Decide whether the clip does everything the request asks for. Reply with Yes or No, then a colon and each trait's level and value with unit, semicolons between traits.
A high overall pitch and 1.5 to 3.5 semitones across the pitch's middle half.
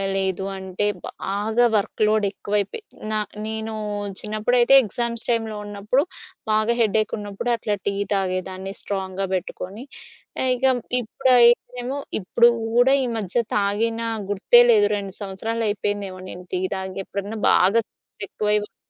Yes: high, 210 Hz; average, 2.8 semitones